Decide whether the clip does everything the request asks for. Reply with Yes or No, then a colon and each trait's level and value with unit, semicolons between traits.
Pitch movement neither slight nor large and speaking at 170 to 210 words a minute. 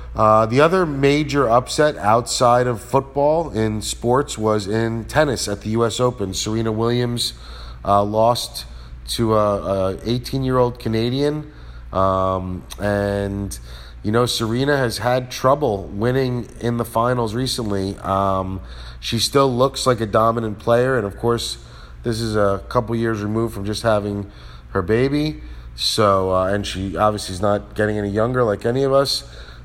No: average, 4.0 semitones; average, 155 wpm